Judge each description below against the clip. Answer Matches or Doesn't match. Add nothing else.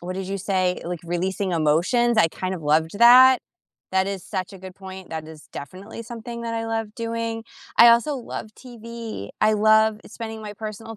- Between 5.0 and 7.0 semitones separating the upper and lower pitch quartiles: Doesn't match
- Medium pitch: Doesn't match